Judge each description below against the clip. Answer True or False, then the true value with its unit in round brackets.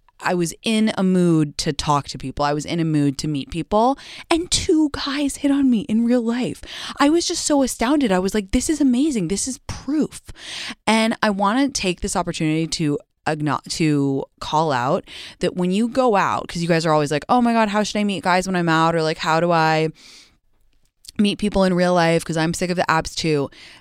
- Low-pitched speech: False (185 Hz)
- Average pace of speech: False (230 wpm)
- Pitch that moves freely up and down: True (7.0 semitones)